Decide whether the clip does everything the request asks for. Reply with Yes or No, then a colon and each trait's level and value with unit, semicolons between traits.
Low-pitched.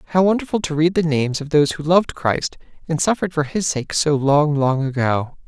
No: medium, 155 Hz